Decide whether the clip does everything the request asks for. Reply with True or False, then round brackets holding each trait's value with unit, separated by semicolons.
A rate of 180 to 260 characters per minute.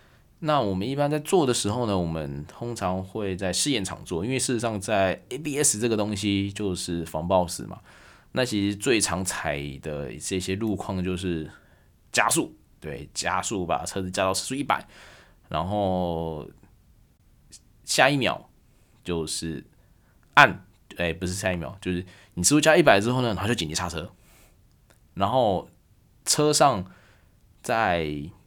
True (220 characters per minute)